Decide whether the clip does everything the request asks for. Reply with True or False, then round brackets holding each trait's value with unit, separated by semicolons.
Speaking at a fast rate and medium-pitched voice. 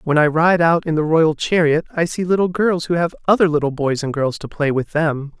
True (255 wpm; 160 Hz)